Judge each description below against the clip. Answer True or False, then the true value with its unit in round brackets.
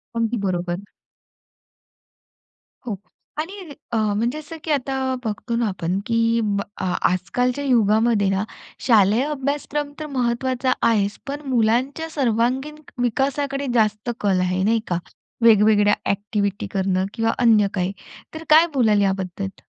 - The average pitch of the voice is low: False (230 Hz)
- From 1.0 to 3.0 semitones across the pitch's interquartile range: False (4.8 semitones)